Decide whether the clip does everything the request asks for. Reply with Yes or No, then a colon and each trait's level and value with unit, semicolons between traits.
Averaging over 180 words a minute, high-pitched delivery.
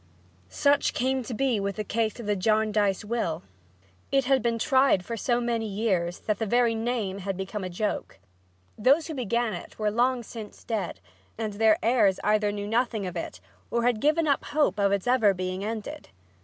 Yes: average, 190 wpm; high, 220 Hz